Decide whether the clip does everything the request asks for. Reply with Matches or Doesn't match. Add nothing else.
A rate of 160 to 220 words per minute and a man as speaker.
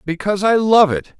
Matches